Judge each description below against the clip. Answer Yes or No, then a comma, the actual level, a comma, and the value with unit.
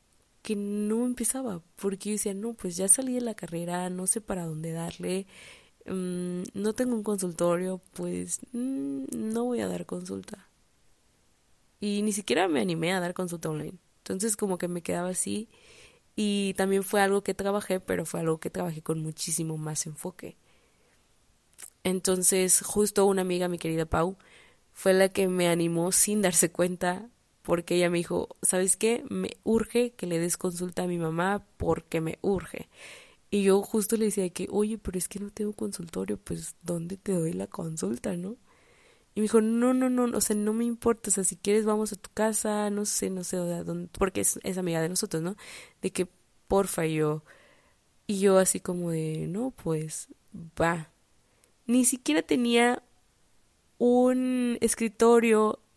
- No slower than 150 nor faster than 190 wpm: Yes, average, 175 wpm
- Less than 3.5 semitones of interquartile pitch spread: No, average, 3.8 semitones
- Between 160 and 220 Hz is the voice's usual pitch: Yes, high, 190 Hz